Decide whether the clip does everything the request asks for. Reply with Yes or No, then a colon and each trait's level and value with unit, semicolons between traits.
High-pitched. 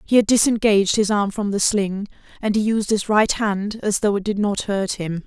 Yes: high, 205 Hz